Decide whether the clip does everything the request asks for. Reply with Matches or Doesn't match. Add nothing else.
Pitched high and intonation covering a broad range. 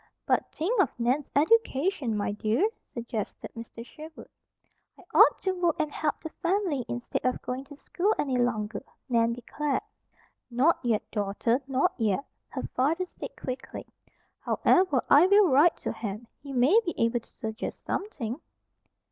Matches